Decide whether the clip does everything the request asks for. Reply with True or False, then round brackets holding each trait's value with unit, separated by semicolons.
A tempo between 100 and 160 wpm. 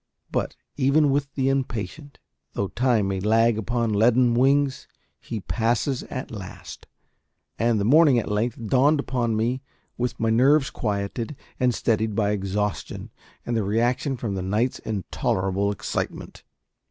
True (140 wpm)